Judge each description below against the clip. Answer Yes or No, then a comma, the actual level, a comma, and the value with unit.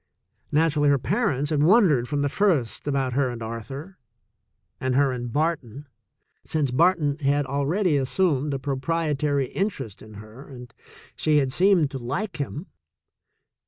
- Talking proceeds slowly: No, average, 150 wpm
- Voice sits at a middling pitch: Yes, medium, 145 Hz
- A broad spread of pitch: No, average, 3.6 semitones